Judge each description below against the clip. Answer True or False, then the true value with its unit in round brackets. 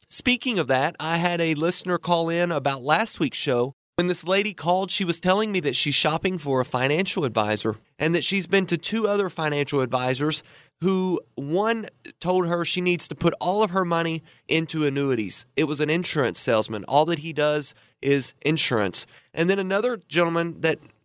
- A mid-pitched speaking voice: True (165 Hz)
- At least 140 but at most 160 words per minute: False (190 wpm)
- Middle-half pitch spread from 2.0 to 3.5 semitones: False (4.4 semitones)